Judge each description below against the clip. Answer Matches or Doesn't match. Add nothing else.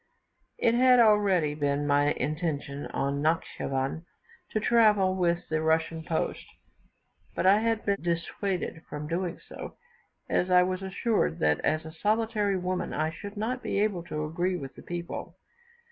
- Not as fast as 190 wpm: Matches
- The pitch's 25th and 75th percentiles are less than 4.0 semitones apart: Doesn't match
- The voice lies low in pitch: Doesn't match